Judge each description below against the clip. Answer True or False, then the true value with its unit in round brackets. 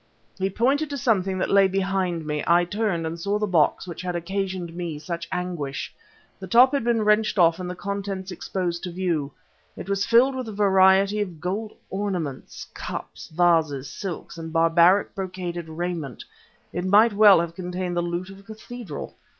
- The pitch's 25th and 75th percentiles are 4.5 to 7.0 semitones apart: False (2.8 semitones)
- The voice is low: False (185 Hz)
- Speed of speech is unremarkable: True (180 wpm)